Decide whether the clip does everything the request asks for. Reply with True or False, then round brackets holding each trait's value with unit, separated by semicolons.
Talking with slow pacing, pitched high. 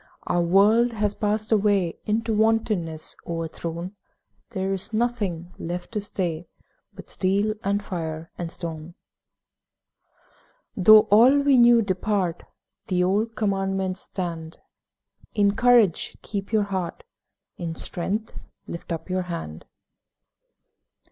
True (115 wpm; 195 Hz)